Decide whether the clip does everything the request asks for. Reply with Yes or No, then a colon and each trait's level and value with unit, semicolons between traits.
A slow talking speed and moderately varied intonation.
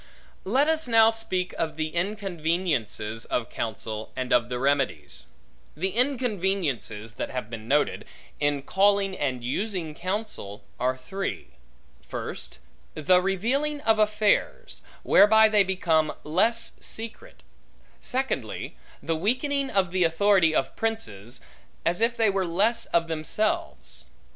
No: slow, 125 wpm; wide, 7.3 semitones